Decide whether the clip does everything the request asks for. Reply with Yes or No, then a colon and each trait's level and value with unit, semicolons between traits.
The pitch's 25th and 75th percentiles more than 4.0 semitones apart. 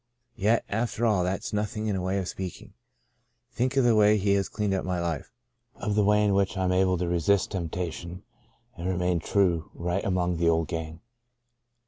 No: average, 3.0 semitones